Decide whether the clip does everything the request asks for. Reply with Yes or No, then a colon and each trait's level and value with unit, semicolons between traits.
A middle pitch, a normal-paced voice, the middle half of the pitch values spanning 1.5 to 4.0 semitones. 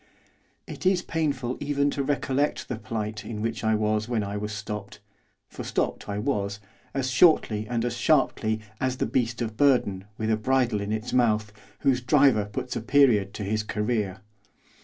No: low, 115 Hz; average, 180 wpm; average, 3.5 semitones